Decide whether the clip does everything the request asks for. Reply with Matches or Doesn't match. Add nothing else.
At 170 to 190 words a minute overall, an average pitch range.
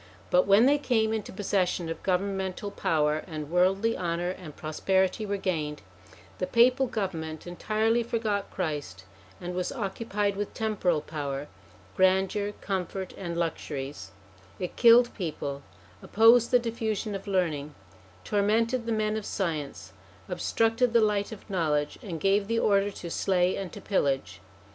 Doesn't match